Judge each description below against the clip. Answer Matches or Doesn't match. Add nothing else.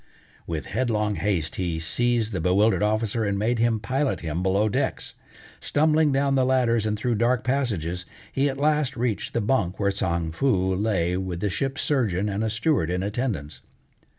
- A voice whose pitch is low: Matches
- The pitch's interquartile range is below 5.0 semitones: Doesn't match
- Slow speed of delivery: Doesn't match